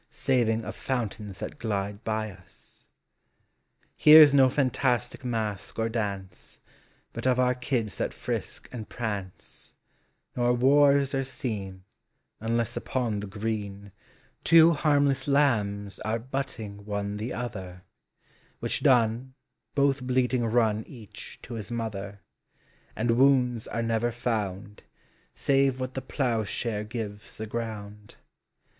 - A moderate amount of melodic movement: Yes, average, 3.7 semitones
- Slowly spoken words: Yes, slow, 125 wpm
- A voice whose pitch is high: No, low, 115 Hz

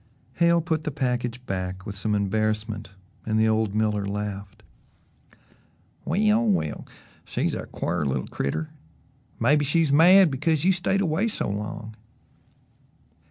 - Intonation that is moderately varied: No, wide, 7.8 semitones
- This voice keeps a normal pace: No, slow, 130 wpm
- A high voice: No, low, 115 Hz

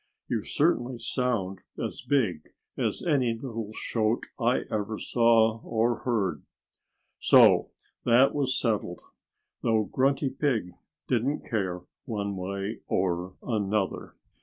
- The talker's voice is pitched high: No, low, 115 Hz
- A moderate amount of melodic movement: Yes, average, 4.0 semitones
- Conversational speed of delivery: No, slow, 110 wpm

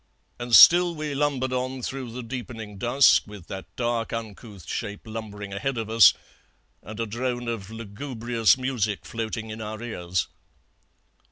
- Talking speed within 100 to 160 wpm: Yes, average, 150 wpm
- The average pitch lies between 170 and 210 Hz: No, low, 115 Hz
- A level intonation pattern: No, average, 3.1 semitones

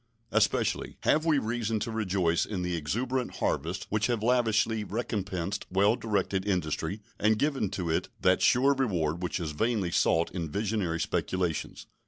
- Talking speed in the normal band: Yes, average, 155 wpm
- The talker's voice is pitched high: No, low, 100 Hz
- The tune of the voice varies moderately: Yes, average, 4.2 semitones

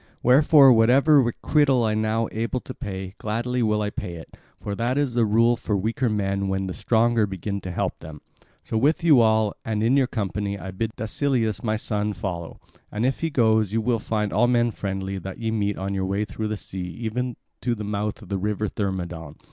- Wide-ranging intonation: No, average, 3.2 semitones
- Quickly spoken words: Yes, fast, 215 wpm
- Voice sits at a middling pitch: No, low, 110 Hz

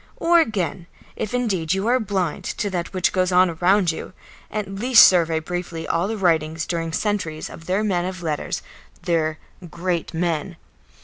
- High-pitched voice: No, medium, 180 Hz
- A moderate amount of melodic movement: Yes, average, 3.3 semitones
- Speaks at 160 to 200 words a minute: Yes, average, 170 wpm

